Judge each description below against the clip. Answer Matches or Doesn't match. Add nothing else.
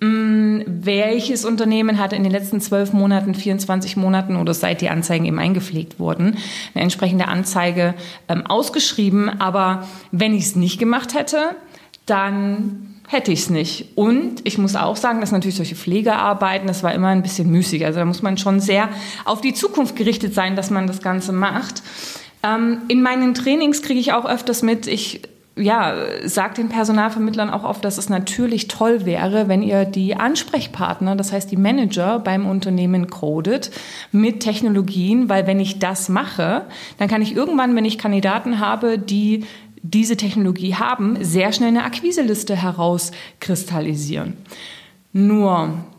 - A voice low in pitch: Doesn't match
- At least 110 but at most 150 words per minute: Doesn't match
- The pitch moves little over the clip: Doesn't match